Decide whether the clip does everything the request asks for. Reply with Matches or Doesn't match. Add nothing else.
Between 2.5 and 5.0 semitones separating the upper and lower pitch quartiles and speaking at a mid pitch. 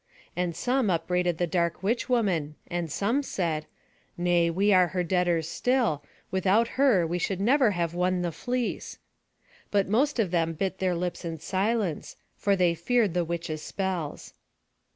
Matches